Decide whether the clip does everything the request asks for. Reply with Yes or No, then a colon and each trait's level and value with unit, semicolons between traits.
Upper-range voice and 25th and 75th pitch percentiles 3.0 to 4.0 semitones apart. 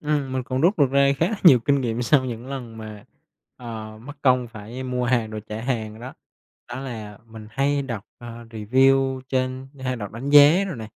No: low, 125 Hz; average, 3.3 semitones